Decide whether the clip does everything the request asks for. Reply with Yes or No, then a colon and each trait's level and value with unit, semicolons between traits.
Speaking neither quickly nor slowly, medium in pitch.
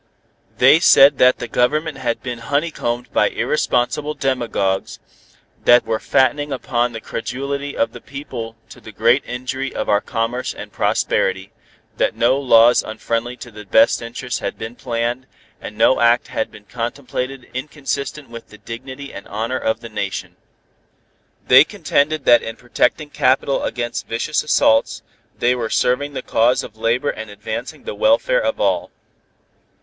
No: average, 155 wpm; low, 125 Hz